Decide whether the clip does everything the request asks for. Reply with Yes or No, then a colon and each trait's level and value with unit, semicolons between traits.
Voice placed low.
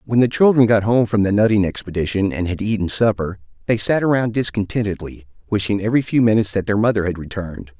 Yes: low, 105 Hz